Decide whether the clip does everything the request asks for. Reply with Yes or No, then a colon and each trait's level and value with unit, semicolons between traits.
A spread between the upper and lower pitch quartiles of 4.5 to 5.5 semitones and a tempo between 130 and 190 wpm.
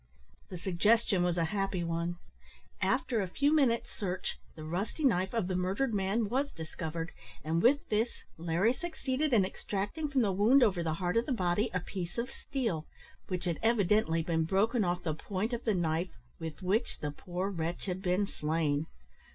Yes: average, 5.1 semitones; average, 185 wpm